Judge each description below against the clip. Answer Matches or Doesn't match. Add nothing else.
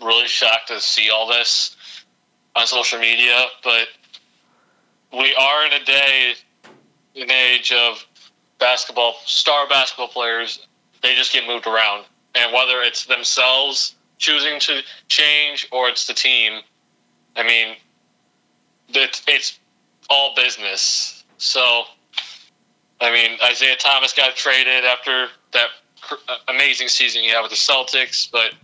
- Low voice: Matches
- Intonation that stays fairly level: Matches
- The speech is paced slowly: Matches